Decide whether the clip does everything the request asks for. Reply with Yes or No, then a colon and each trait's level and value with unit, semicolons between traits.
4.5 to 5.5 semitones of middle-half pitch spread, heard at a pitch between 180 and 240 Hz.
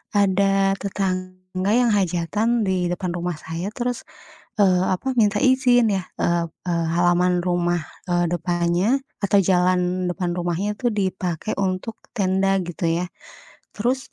No: narrow, 2.6 semitones; medium, 185 Hz